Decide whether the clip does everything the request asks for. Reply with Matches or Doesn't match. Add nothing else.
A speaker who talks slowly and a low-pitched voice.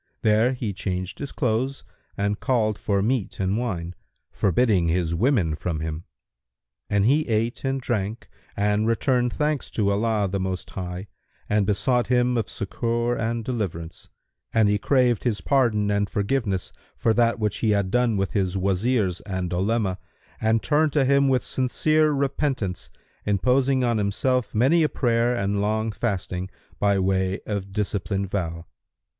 Doesn't match